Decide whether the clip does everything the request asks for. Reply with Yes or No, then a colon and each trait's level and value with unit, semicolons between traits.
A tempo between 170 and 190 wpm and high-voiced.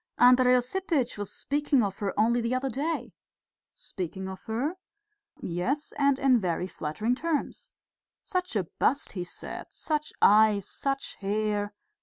No: average, 140 wpm; high, 240 Hz